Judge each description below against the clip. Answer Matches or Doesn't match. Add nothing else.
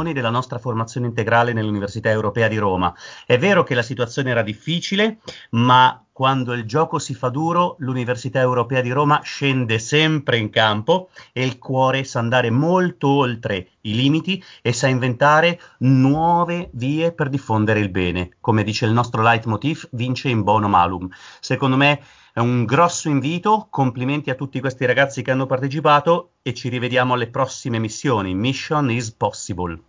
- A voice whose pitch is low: Matches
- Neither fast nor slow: Matches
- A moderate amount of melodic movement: Matches